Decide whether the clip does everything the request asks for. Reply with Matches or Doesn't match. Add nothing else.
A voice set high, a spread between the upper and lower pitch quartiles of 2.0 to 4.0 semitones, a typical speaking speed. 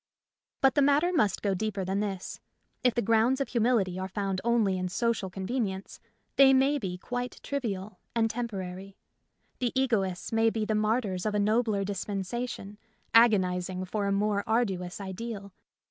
Matches